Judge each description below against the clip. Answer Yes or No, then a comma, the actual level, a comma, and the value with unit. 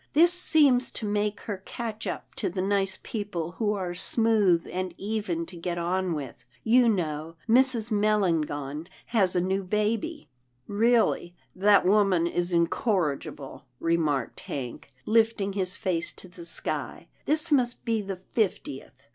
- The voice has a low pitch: No, high, 195 Hz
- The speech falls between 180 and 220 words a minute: No, average, 160 wpm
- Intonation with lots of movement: No, average, 4.5 semitones